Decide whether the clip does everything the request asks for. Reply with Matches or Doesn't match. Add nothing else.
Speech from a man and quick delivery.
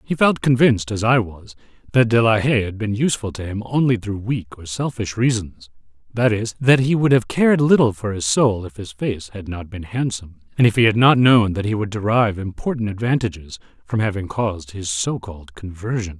Matches